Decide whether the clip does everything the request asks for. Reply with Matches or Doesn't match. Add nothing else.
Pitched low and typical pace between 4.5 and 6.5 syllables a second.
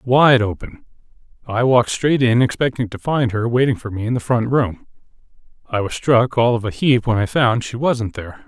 Matches